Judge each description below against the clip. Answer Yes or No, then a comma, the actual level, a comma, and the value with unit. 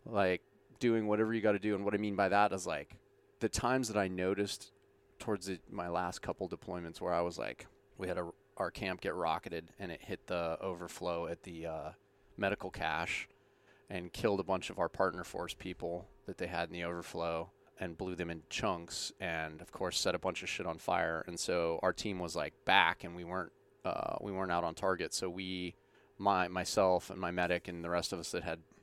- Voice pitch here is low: Yes, very low, 90 Hz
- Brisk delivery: Yes, fast, 225 wpm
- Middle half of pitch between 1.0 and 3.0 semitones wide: Yes, narrow, 2.6 semitones